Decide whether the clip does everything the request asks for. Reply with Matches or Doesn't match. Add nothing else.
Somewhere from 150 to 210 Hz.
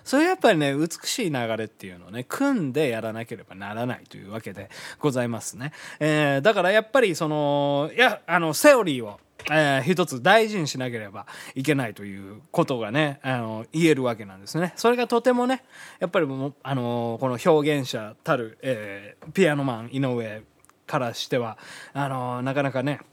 Doesn't match